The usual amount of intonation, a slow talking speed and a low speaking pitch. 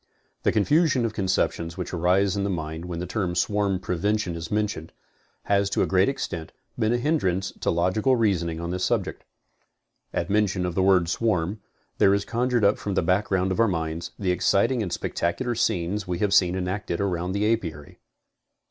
No: average, 3.3 semitones; average, 185 wpm; very low, 95 Hz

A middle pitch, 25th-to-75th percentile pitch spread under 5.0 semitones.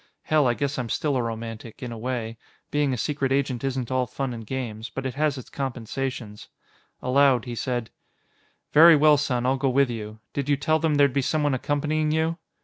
No: low, 130 Hz; average, 3.1 semitones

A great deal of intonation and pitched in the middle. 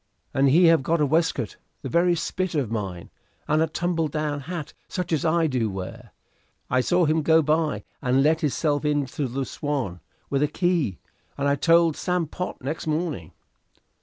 No: average, 3.5 semitones; medium, 150 Hz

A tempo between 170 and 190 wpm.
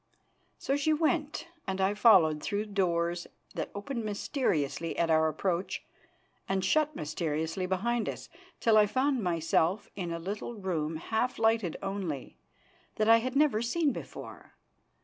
No: average, 145 wpm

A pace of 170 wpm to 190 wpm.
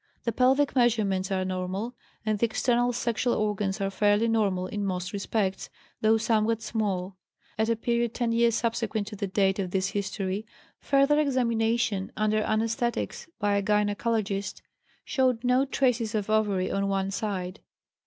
No: average, 155 wpm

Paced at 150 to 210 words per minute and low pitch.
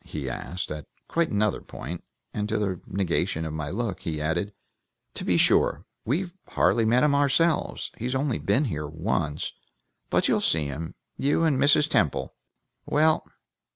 Yes: average, 160 wpm; low, 105 Hz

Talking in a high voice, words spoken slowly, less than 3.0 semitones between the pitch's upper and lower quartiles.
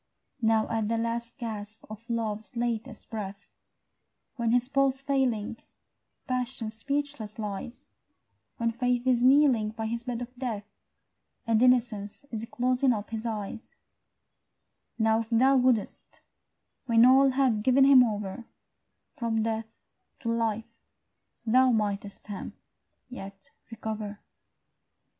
Yes: high, 230 Hz; slow, 120 wpm; narrow, 2.5 semitones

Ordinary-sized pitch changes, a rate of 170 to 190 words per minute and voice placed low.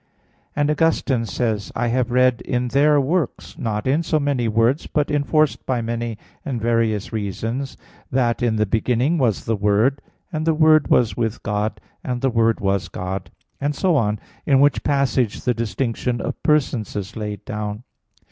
Yes: average, 4.3 semitones; average, 180 wpm; low, 120 Hz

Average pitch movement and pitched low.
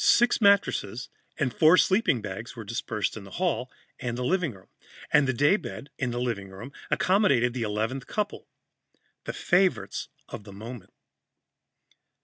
No: wide, 8.0 semitones; low, 125 Hz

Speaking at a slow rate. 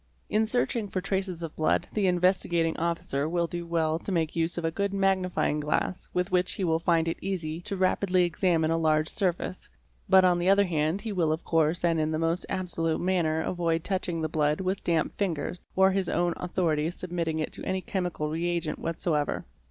No: fast, 205 wpm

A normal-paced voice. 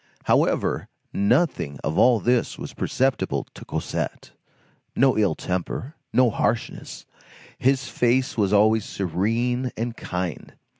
No: slow, 115 wpm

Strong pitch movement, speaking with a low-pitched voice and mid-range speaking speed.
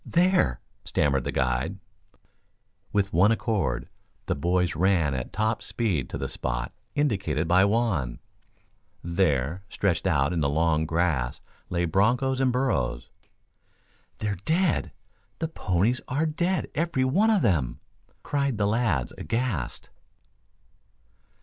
No: wide, 8.3 semitones; very low, 95 Hz; slow, 125 wpm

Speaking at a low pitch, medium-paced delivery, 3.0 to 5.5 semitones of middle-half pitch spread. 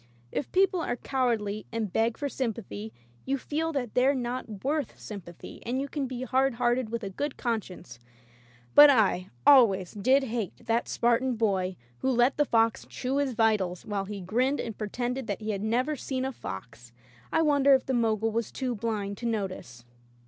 No: high, 235 Hz; average, 190 wpm; average, 4.1 semitones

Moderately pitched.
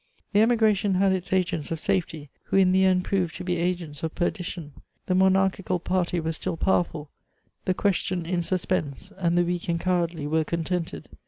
Yes: medium, 180 Hz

